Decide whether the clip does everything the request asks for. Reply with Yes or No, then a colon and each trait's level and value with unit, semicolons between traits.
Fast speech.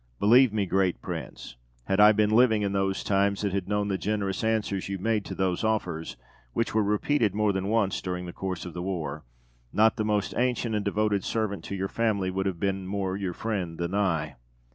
Yes: fast, 210 wpm